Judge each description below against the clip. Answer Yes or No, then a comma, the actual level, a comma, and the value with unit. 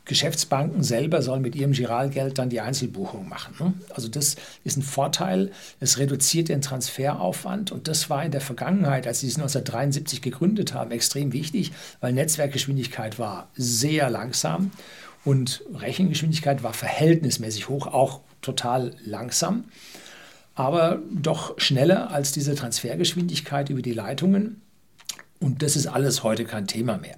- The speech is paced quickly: No, average, 140 wpm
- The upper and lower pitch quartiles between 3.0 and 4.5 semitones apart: Yes, average, 3.7 semitones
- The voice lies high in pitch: No, medium, 140 Hz